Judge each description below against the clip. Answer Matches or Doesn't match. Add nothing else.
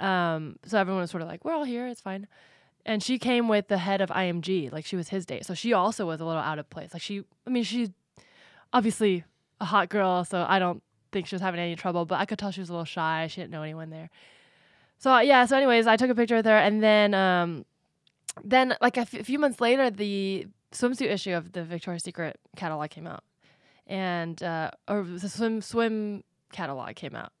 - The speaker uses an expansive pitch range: Doesn't match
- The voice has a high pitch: Matches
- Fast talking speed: Matches